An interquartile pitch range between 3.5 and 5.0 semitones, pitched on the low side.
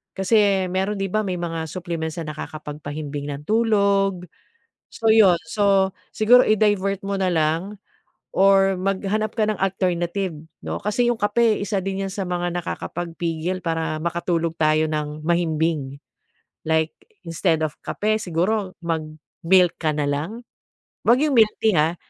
No: average, 3.9 semitones; medium, 185 Hz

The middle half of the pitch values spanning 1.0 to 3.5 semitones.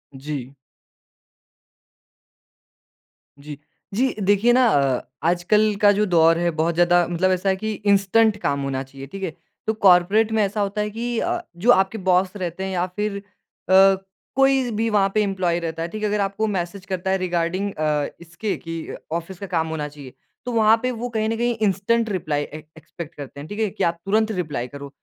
No: average, 4.2 semitones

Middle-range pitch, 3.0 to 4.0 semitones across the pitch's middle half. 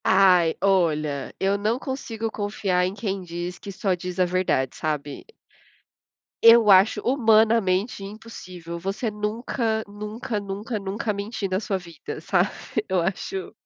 No: high, 195 Hz; average, 3.3 semitones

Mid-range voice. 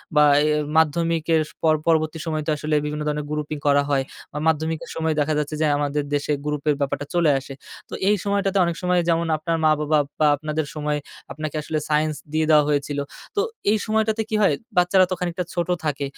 Yes: medium, 155 Hz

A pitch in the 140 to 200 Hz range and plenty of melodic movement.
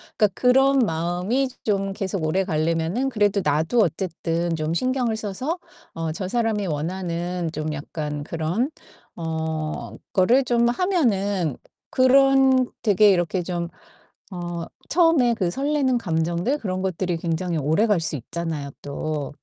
Yes: medium, 185 Hz; wide, 6.5 semitones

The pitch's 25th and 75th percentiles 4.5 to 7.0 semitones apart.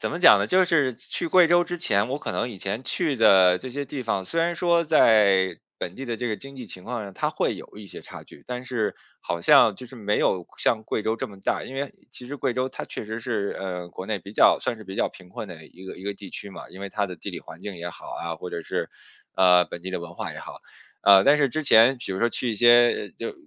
Yes: wide, 5.5 semitones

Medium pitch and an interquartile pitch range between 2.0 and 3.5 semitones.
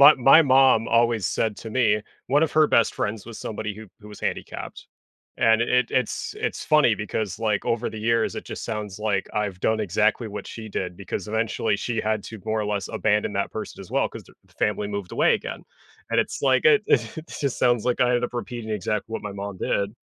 No: low, 110 Hz; narrow, 2.5 semitones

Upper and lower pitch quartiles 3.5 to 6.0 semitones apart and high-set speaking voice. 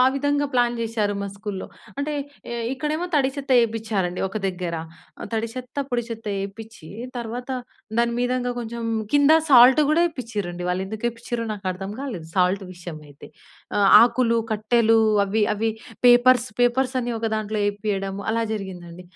Yes: average, 3.9 semitones; high, 225 Hz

